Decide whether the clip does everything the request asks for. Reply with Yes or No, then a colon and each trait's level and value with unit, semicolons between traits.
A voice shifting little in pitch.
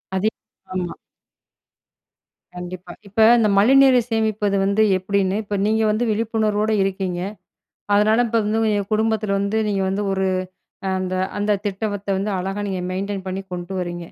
Yes: narrow, 2.3 semitones